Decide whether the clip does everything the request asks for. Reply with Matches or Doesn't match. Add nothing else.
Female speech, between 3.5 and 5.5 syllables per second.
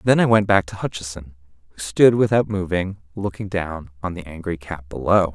Doesn't match